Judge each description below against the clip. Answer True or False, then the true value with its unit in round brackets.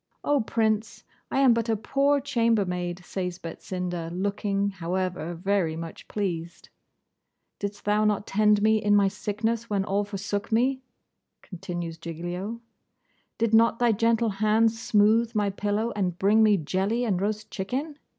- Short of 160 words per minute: True (145 wpm)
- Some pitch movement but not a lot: True (3.2 semitones)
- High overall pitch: True (205 Hz)